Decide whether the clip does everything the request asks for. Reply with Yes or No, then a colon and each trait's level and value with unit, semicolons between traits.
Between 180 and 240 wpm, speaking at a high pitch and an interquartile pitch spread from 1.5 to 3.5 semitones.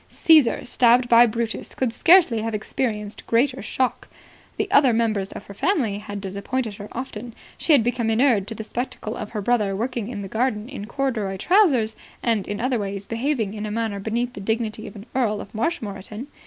Yes: average, 195 wpm; high, 225 Hz; average, 3.1 semitones